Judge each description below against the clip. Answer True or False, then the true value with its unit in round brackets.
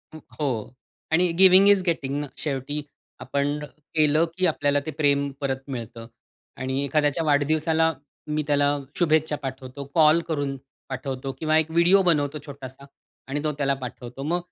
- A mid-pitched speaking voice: True (145 Hz)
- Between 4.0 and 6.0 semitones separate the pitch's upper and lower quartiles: False (2.4 semitones)